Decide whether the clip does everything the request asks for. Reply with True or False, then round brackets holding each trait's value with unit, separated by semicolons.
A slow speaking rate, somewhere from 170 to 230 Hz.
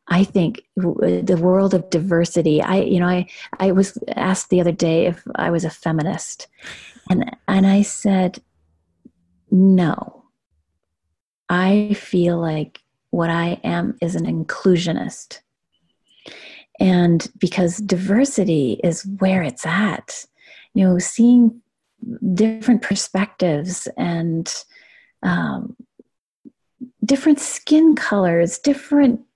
True (110 wpm; 185 Hz)